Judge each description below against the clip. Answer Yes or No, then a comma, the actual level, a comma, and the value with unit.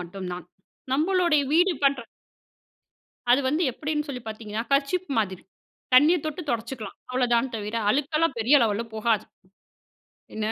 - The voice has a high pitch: Yes, very high, 255 Hz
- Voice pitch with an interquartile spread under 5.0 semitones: No, wide, 5.6 semitones